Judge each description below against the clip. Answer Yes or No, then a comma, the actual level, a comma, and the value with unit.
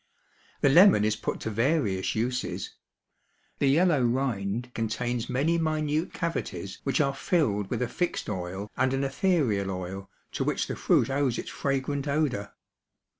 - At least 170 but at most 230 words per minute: No, average, 150 wpm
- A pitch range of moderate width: No, wide, 5.9 semitones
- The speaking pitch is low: Yes, low, 130 Hz